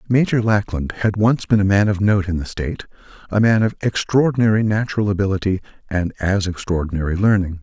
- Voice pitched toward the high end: No, low, 100 Hz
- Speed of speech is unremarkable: Yes, average, 165 wpm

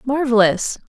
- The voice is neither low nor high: No, high, 235 Hz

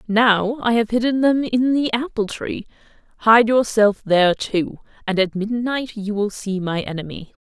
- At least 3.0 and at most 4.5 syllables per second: Yes, 4.4 syllables/s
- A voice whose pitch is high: Yes, high, 220 Hz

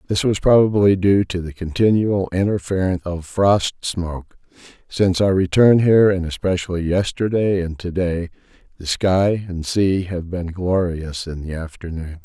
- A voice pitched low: Yes, very low, 90 Hz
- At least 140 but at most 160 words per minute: Yes, average, 150 wpm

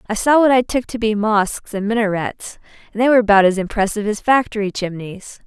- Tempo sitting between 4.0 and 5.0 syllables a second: No, 5.9 syllables/s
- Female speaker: Yes, female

